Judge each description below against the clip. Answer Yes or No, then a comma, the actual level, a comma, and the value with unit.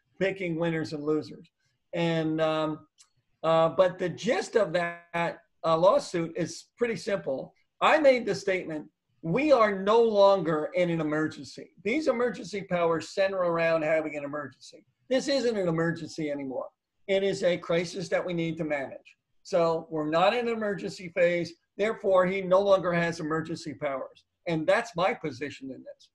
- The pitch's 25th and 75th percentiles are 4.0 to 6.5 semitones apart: No, average, 3.6 semitones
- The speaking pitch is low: No, medium, 170 Hz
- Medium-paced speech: Yes, average, 160 wpm